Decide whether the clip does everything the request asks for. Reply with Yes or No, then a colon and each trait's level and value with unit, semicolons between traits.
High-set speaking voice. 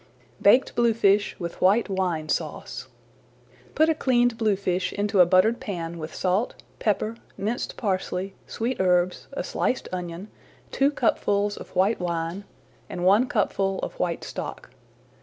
Yes: high, 195 Hz